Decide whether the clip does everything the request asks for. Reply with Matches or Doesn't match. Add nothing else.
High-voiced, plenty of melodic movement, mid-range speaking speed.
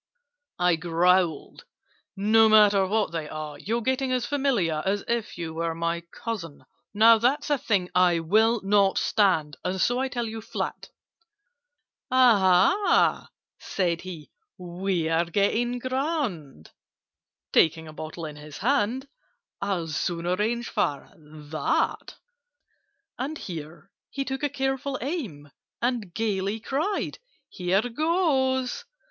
Doesn't match